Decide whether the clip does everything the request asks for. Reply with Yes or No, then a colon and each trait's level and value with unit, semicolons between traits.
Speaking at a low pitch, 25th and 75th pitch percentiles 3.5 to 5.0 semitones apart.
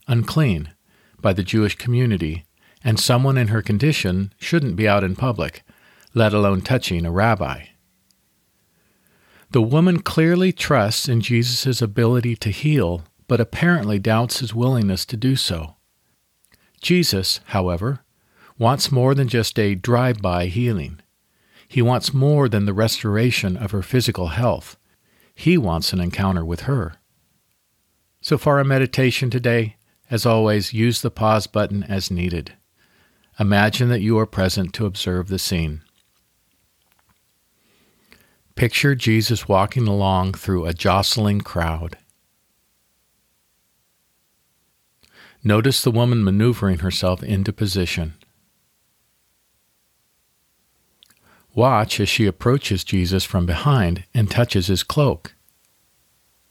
Yes: low, 105 Hz; average, 4.6 semitones